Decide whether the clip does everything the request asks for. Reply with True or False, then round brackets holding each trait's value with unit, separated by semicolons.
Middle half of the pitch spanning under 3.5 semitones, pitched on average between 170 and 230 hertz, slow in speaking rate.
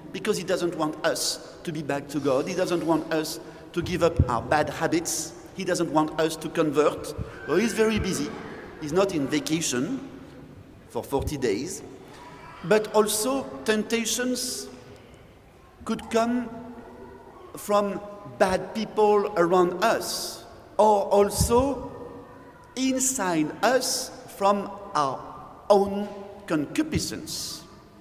False (5.2 semitones; 190 Hz; 120 wpm)